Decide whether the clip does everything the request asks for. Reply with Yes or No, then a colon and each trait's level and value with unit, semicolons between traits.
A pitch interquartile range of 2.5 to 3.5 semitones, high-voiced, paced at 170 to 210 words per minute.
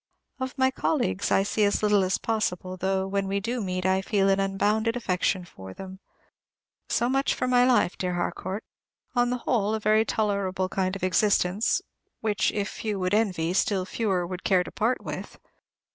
Yes: average, 2.9 semitones; high, 200 Hz; average, 185 wpm